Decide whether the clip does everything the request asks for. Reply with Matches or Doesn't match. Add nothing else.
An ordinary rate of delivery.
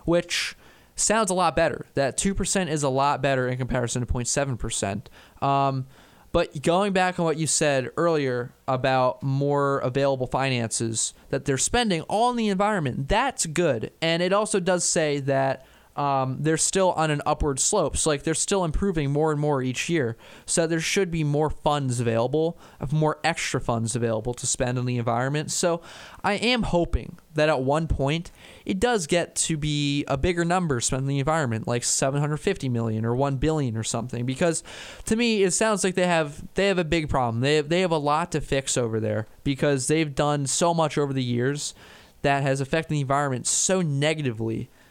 Matches